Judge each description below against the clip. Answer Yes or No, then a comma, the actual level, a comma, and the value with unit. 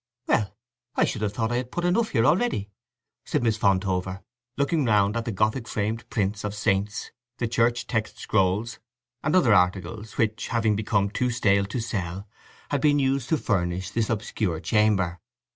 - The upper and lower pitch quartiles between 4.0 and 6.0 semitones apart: No, average, 3.2 semitones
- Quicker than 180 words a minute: No, average, 175 wpm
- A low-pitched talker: Yes, low, 110 Hz